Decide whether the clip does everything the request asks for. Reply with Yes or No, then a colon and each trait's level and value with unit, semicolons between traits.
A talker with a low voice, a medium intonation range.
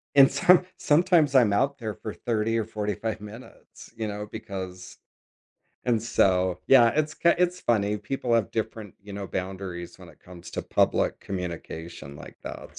Yes: low, 105 Hz; average, 4.6 semitones